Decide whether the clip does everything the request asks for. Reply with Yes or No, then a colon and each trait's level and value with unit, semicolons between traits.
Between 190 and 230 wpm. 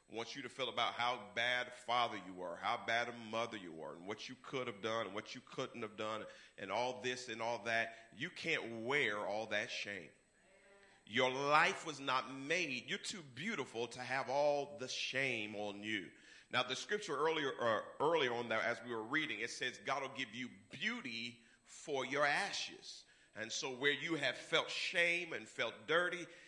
Yes: average, 200 wpm